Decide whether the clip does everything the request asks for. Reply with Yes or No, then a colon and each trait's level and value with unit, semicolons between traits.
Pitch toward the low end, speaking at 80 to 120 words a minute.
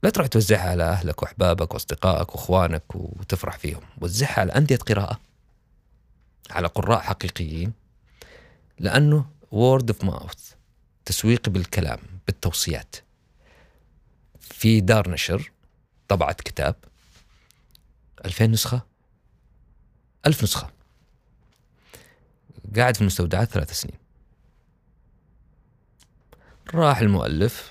Yes: low, 100 Hz; average, 85 wpm